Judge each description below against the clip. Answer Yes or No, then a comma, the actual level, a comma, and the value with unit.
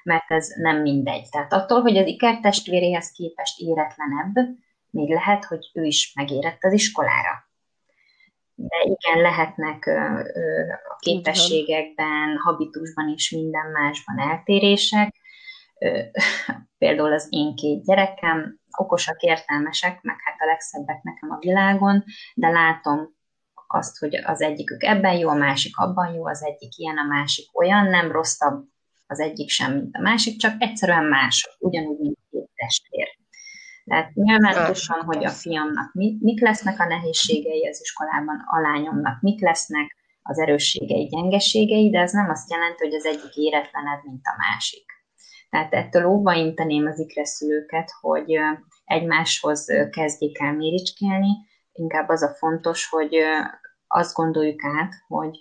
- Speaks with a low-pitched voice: No, medium, 165 Hz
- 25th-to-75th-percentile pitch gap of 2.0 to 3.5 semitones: No, average, 4.5 semitones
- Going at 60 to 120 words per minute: No, average, 135 wpm